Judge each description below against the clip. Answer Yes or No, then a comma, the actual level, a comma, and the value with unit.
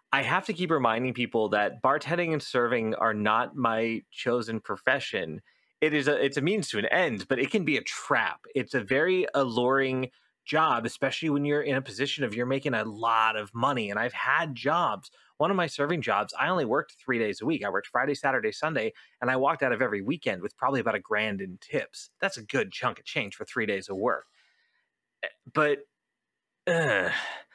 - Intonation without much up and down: No, average, 4.7 semitones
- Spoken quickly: Yes, fast, 210 wpm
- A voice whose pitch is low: Yes, low, 130 Hz